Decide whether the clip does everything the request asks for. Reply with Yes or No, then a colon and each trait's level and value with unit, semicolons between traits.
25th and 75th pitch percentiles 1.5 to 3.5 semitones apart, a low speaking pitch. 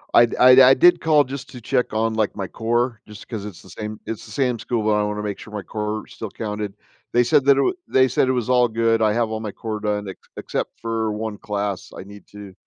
Yes: narrow, 2.6 semitones; low, 110 Hz